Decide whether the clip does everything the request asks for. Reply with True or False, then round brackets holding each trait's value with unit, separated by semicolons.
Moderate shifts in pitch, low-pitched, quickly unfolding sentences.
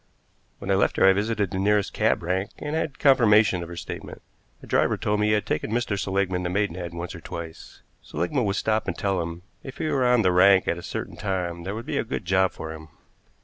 True (3.6 semitones; 95 Hz; 240 wpm)